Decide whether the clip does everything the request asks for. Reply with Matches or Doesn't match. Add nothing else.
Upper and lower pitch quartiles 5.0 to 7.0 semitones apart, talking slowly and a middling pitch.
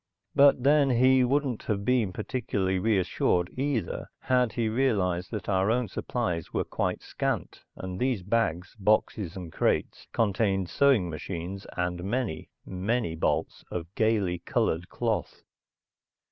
Doesn't match